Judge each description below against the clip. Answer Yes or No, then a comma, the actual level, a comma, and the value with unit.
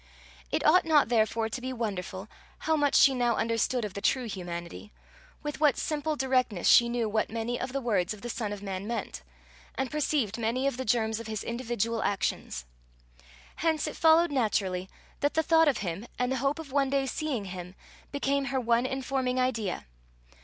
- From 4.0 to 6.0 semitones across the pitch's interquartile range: Yes, average, 4.3 semitones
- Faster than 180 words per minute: Yes, average, 190 wpm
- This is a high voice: Yes, high, 240 Hz